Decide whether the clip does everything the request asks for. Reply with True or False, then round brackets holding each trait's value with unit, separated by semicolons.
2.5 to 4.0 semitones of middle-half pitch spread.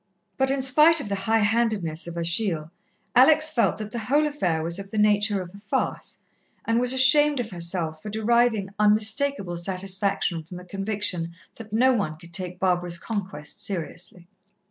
False (5.0 semitones)